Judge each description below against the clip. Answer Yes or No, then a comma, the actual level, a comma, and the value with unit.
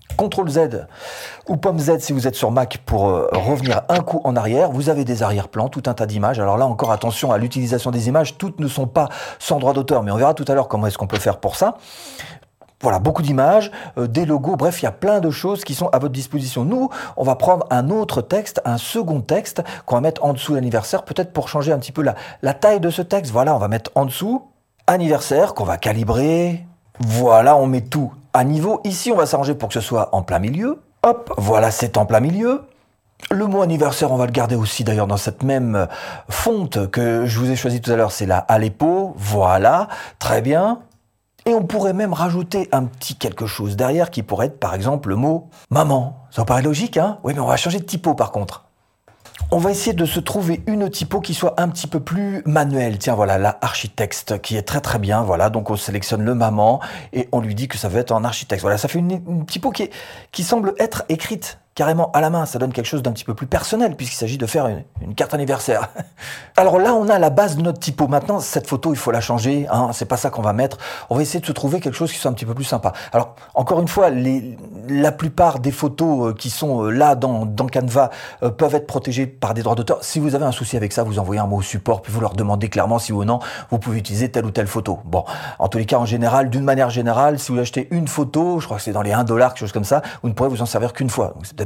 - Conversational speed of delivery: No, fast, 255 wpm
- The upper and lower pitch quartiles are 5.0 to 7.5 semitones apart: Yes, wide, 5.6 semitones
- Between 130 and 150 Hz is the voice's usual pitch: Yes, low, 135 Hz